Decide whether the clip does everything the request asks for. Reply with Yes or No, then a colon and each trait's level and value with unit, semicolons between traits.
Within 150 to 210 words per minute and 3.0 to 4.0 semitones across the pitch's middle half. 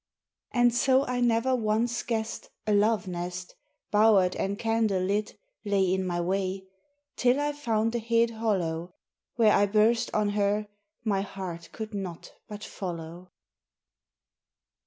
No: slow, 135 wpm; average, 3.4 semitones